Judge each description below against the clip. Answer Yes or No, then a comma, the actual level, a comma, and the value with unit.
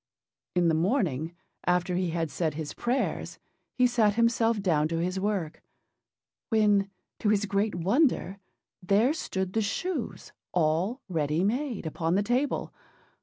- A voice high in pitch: Yes, high, 195 Hz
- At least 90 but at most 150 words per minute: Yes, average, 140 wpm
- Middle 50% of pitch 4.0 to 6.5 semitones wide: Yes, average, 5.0 semitones